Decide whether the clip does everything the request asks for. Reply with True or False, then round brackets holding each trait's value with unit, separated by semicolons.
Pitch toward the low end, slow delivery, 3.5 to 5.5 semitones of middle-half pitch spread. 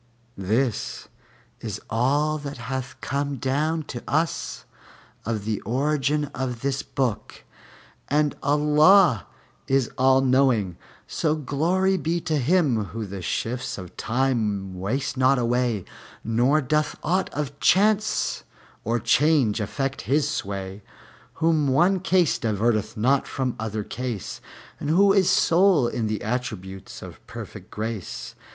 True (130 Hz; 130 wpm; 5.0 semitones)